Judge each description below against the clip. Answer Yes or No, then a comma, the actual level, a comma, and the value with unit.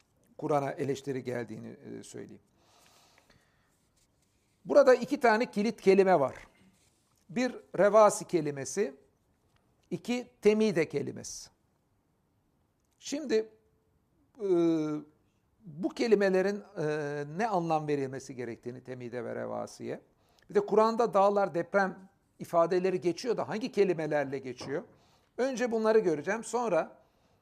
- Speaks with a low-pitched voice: No, medium, 175 Hz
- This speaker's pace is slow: Yes, slow, 90 wpm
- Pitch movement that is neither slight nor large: No, wide, 7.4 semitones